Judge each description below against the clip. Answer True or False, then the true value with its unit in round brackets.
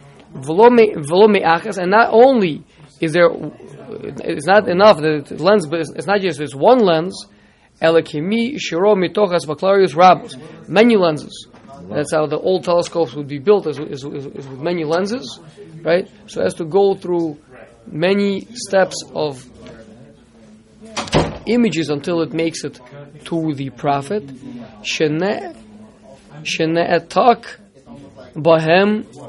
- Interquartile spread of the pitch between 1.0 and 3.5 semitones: False (4.9 semitones)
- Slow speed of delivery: True (120 wpm)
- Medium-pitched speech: True (165 Hz)